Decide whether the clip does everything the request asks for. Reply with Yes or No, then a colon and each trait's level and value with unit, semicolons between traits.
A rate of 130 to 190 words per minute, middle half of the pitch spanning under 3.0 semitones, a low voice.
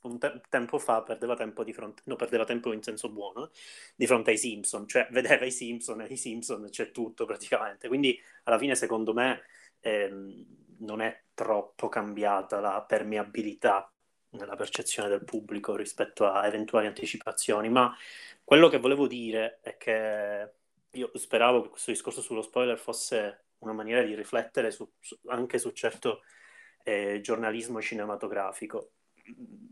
Yes: average, 155 wpm; narrow, 2.5 semitones; low, 110 Hz